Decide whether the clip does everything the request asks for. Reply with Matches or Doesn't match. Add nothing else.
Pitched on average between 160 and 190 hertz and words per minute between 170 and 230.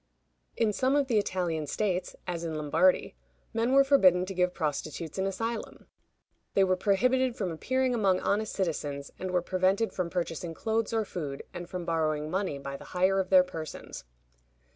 Matches